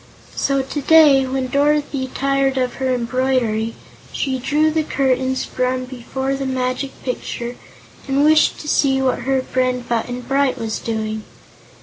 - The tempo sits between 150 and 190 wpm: No, average, 140 wpm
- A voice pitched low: No, very high, 260 Hz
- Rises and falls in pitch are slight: Yes, narrow, 1.5 semitones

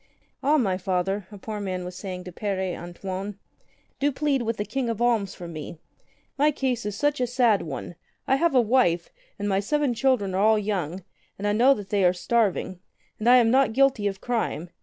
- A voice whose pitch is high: Yes, high, 210 Hz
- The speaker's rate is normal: No, fast, 210 wpm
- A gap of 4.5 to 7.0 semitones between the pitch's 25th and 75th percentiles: Yes, average, 4.9 semitones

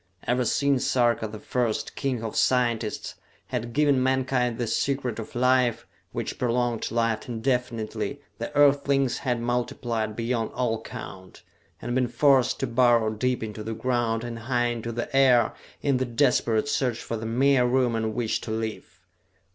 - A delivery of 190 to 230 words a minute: No, average, 160 wpm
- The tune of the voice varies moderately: No, narrow, 2.2 semitones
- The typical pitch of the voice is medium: No, low, 120 Hz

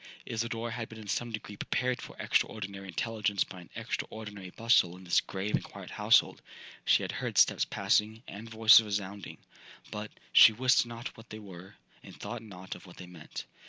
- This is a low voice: Yes, low, 105 Hz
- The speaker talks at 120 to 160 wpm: No, average, 185 wpm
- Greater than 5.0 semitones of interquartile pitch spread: No, average, 2.8 semitones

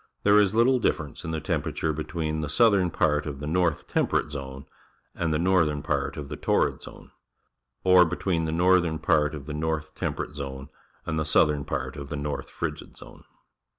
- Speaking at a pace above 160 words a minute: Yes, average, 185 wpm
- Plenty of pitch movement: No, average, 2.9 semitones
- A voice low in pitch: Yes, very low, 80 Hz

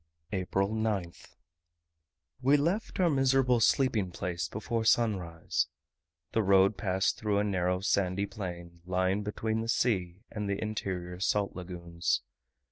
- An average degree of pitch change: Yes, average, 3.5 semitones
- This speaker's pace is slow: Yes, slow, 125 wpm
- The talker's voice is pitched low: Yes, low, 100 Hz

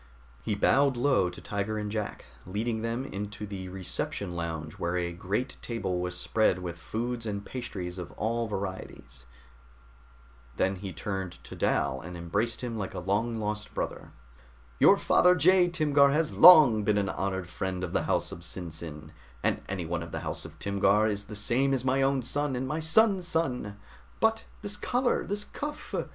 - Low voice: Yes, low, 105 Hz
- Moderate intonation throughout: No, wide, 6.2 semitones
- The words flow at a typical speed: Yes, average, 175 wpm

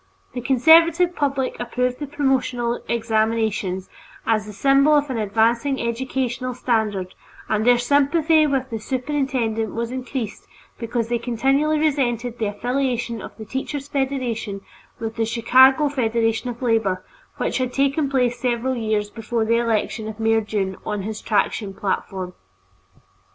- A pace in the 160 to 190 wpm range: No, average, 140 wpm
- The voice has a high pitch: Yes, high, 240 Hz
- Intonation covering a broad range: No, average, 3.3 semitones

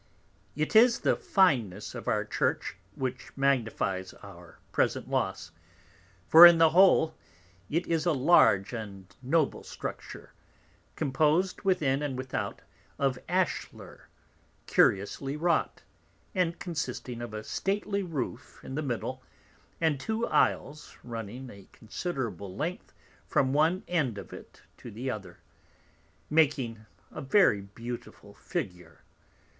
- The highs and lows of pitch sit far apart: Yes, wide, 6.8 semitones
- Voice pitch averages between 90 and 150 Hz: Yes, low, 135 Hz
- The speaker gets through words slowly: Yes, slow, 120 wpm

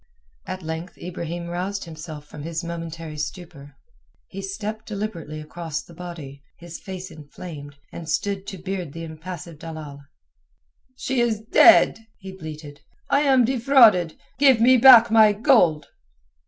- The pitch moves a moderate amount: Yes, average, 4.9 semitones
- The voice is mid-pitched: Yes, medium, 175 Hz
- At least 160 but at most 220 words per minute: No, average, 140 wpm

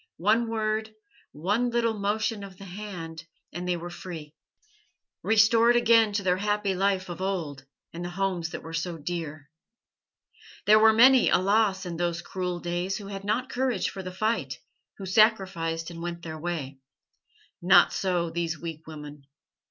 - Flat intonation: No, average, 4.0 semitones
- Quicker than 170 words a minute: No, average, 160 wpm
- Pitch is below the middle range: No, medium, 185 Hz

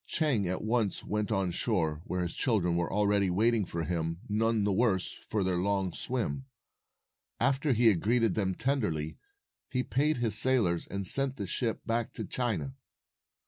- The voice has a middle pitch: No, low, 105 Hz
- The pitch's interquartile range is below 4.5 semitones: No, average, 4.8 semitones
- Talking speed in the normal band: Yes, average, 170 wpm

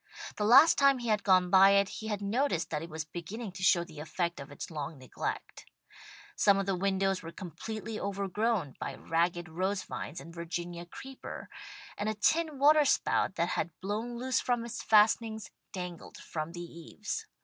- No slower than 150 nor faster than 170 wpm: No, average, 180 wpm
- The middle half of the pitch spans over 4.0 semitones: Yes, average, 4.4 semitones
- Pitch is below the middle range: No, high, 195 Hz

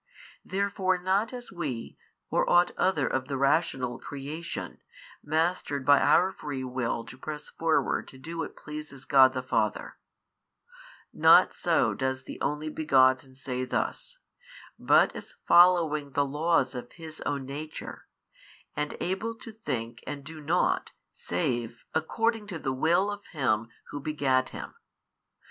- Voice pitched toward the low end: No, medium, 150 Hz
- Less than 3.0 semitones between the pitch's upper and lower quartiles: No, average, 4.7 semitones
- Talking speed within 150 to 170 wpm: No, average, 140 wpm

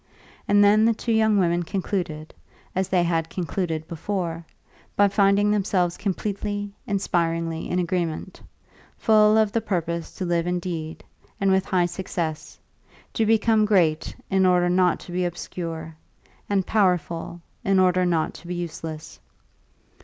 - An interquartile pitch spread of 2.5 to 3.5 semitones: Yes, average, 3.1 semitones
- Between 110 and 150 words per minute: Yes, average, 140 wpm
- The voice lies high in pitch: No, medium, 180 Hz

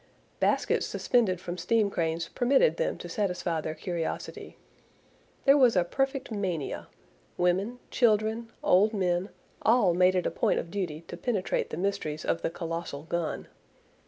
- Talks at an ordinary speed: Yes, average, 150 wpm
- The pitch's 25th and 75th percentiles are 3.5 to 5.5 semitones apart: Yes, average, 4.8 semitones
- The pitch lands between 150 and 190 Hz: Yes, medium, 185 Hz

